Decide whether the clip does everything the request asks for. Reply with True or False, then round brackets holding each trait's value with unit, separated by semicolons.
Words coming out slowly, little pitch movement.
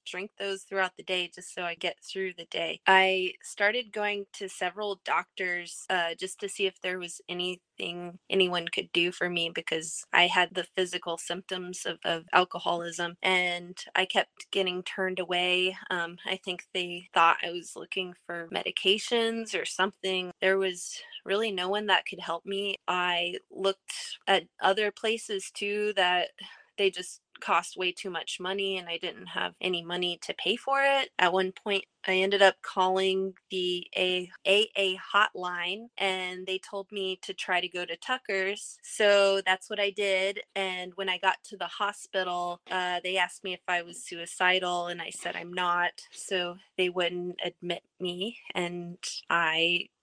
False (175 wpm; 1.7 semitones)